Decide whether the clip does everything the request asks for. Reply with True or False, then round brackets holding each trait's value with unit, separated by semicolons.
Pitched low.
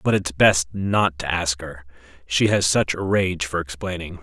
True (85 Hz)